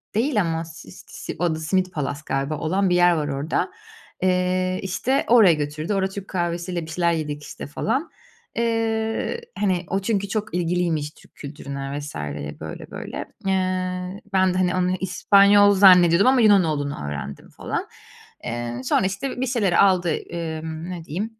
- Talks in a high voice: No, medium, 180 Hz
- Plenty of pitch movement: No, average, 3.8 semitones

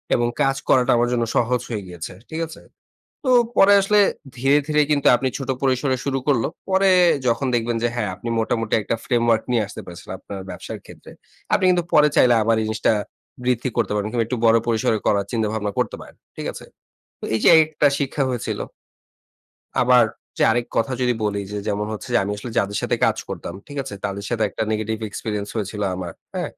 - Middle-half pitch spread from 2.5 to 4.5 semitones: Yes, average, 3.7 semitones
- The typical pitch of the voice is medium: No, low, 115 Hz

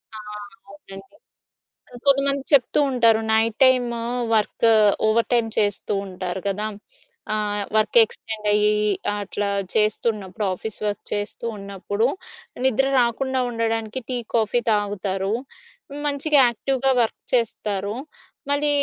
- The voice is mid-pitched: No, high, 220 Hz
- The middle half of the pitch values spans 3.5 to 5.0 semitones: No, average, 2.9 semitones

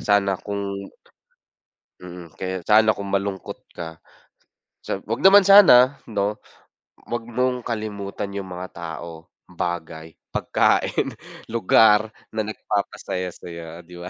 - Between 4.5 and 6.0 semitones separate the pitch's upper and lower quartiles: No, average, 3.6 semitones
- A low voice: Yes, low, 100 Hz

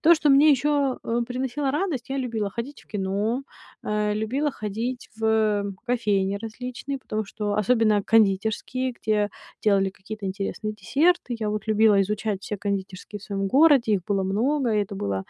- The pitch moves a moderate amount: Yes, average, 3.9 semitones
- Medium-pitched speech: No, high, 215 Hz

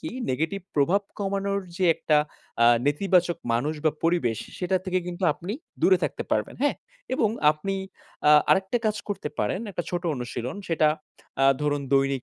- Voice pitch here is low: No, medium, 175 Hz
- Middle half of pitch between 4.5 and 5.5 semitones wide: Yes, average, 5.0 semitones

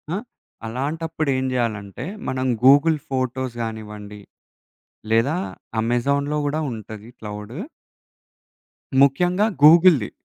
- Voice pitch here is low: Yes, low, 130 Hz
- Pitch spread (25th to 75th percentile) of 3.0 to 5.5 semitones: Yes, average, 5.2 semitones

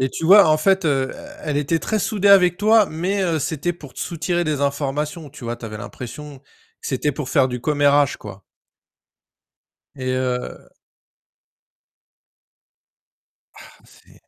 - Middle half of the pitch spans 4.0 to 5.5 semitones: Yes, average, 4.7 semitones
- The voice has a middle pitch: Yes, medium, 150 Hz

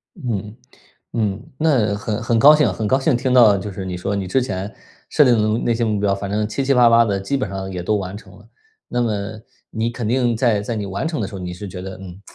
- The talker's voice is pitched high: No, low, 105 Hz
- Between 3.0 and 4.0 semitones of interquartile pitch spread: Yes, average, 3.6 semitones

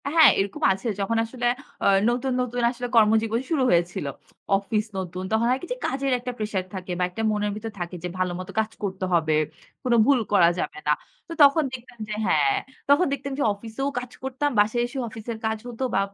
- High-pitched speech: Yes, high, 225 Hz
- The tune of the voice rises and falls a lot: No, average, 4.5 semitones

